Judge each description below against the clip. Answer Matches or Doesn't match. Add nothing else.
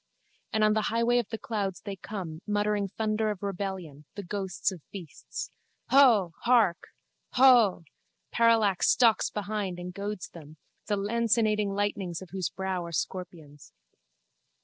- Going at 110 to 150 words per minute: Matches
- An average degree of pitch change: Matches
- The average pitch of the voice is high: Matches